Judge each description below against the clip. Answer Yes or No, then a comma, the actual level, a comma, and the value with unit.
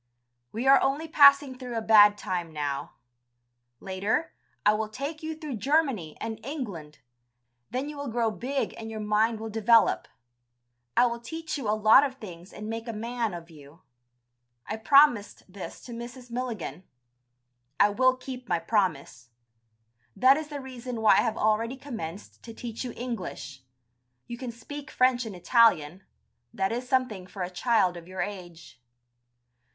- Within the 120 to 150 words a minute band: No, average, 165 wpm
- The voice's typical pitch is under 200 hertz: No, high, 225 Hz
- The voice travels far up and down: No, average, 4.6 semitones